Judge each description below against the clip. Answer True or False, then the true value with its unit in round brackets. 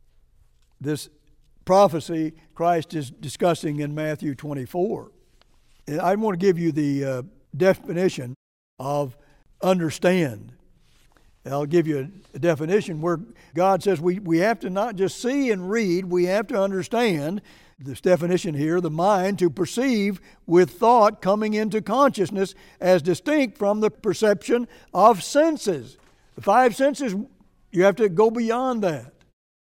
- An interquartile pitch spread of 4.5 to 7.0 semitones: True (5.1 semitones)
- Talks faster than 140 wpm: False (135 wpm)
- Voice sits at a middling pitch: True (180 Hz)